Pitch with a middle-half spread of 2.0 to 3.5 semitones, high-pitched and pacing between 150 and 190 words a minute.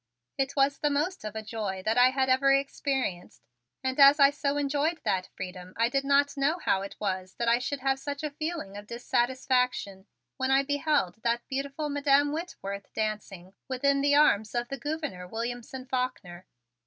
No: average, 4.7 semitones; very high, 265 Hz; average, 180 wpm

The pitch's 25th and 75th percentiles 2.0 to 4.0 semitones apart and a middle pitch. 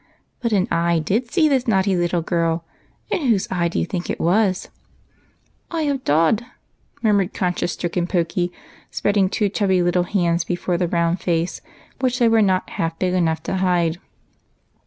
Yes: average, 3.3 semitones; medium, 180 Hz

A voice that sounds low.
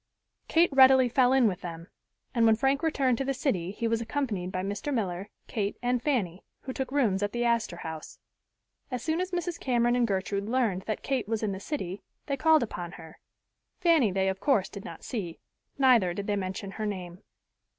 No: high, 230 Hz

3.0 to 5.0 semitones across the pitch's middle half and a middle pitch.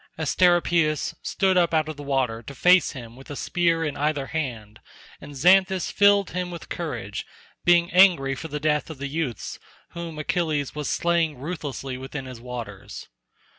Yes: average, 4.2 semitones; medium, 155 Hz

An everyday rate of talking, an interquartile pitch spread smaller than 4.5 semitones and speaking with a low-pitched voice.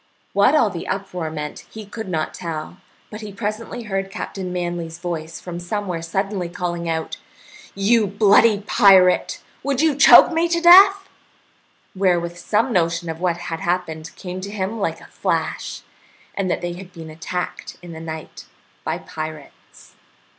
No: average, 160 wpm; average, 3.6 semitones; medium, 185 Hz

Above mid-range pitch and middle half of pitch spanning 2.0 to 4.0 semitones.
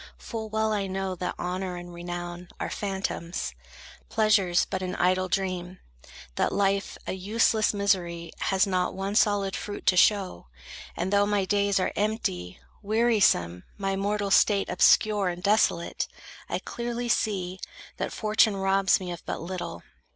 Yes: high, 195 Hz; narrow, 2.4 semitones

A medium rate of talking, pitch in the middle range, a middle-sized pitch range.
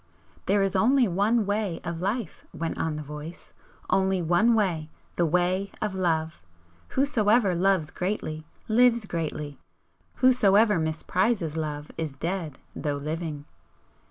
No: slow, 130 wpm; medium, 180 Hz; average, 4.7 semitones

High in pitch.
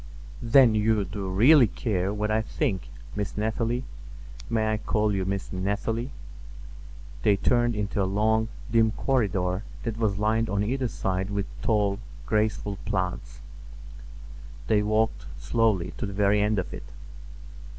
No: low, 105 Hz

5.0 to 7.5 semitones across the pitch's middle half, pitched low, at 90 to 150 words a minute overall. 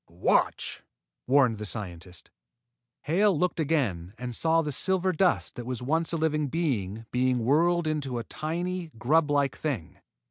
No: wide, 5.5 semitones; medium, 145 Hz; average, 145 wpm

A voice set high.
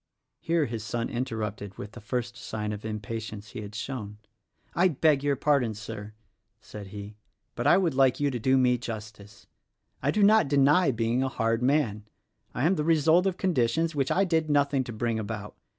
No: low, 120 Hz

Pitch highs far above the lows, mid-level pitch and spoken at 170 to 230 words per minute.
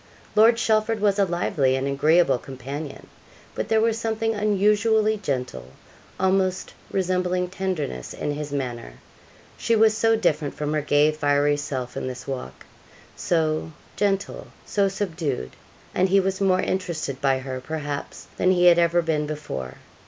No: wide, 5.7 semitones; medium, 170 Hz; average, 150 wpm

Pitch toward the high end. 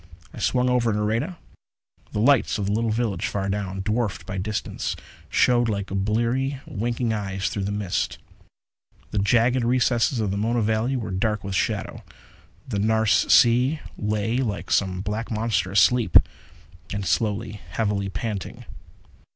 No: low, 110 Hz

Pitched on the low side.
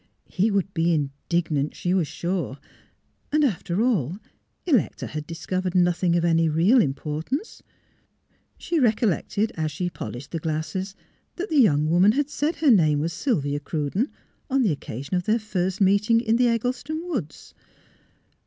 No: medium, 180 Hz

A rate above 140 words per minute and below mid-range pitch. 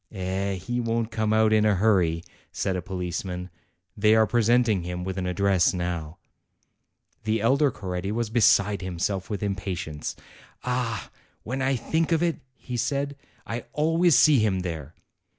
Yes: average, 160 wpm; low, 105 Hz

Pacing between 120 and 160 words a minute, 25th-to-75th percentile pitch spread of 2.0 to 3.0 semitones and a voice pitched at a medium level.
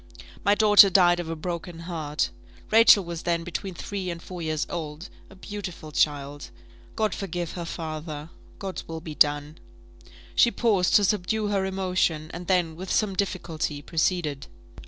No: average, 155 wpm; average, 3.4 semitones; medium, 175 Hz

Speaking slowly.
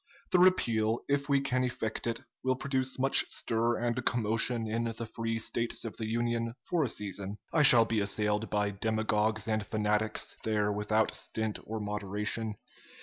No: average, 165 wpm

